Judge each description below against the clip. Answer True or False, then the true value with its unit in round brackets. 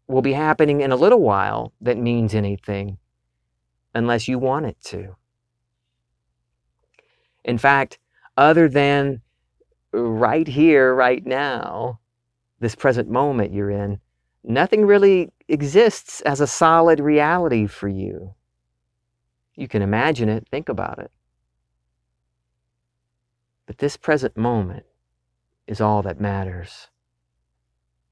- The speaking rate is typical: False (110 wpm)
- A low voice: True (115 Hz)